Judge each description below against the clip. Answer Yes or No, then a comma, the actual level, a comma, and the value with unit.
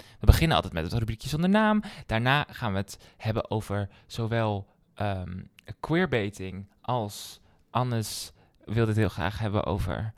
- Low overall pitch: Yes, low, 105 Hz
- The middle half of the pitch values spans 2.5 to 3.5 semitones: Yes, average, 3.0 semitones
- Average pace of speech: Yes, average, 145 wpm